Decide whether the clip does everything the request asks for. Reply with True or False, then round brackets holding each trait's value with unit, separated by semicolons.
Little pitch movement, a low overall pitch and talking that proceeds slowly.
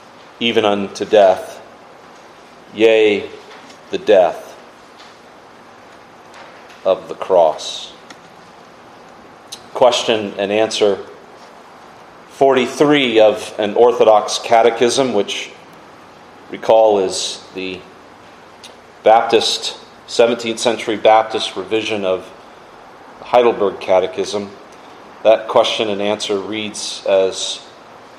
True (2.2 semitones; 110 Hz; 75 wpm)